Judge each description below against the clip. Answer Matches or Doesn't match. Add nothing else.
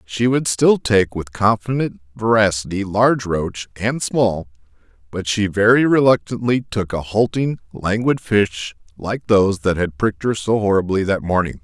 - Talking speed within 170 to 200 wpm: Doesn't match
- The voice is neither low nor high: Doesn't match